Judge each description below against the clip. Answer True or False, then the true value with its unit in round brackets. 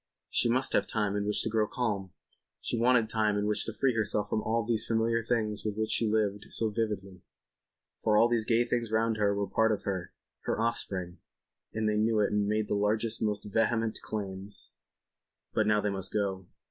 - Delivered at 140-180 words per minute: False (200 wpm)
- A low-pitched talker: True (110 Hz)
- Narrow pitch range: True (1.7 semitones)